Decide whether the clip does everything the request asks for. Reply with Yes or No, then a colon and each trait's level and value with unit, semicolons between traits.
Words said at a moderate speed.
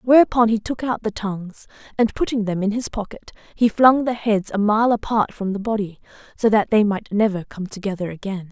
No: fast, 210 wpm